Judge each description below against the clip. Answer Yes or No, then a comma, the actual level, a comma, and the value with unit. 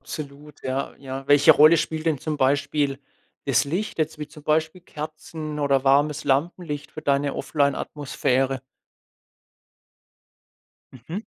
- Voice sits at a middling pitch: Yes, medium, 145 Hz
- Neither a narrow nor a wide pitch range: No, narrow, 2.1 semitones